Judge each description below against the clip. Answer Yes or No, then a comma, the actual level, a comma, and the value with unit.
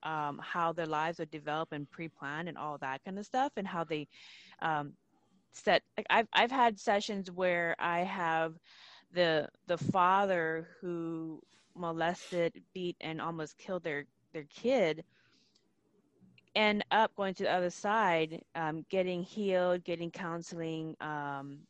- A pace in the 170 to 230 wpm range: No, average, 140 wpm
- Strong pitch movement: No, average, 2.9 semitones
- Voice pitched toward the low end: No, medium, 170 Hz